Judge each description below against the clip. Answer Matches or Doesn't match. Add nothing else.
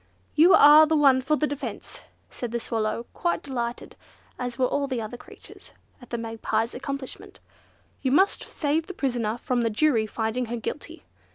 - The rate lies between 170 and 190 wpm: Matches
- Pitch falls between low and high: Doesn't match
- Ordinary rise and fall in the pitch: Matches